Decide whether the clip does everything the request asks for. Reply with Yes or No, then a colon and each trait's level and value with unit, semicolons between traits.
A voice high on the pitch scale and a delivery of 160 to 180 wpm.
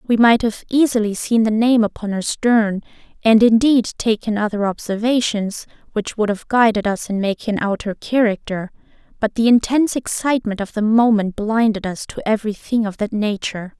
Yes: high, 220 Hz; average, 175 wpm